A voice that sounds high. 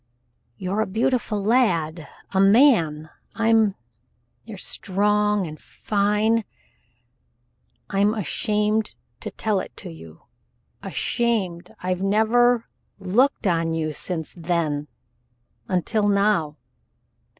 Yes: high, 200 Hz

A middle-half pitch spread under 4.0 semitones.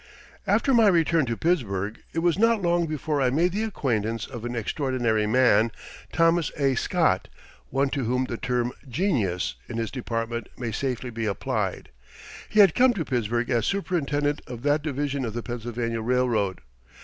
No: wide, 5.4 semitones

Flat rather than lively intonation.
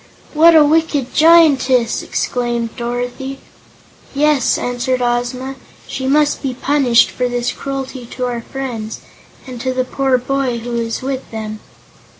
Yes: narrow, 2.1 semitones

